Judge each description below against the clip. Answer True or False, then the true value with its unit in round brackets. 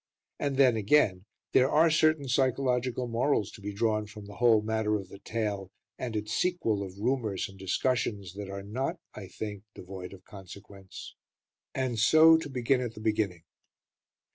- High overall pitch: False (110 Hz)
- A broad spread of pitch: False (4.4 semitones)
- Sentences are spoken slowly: False (165 wpm)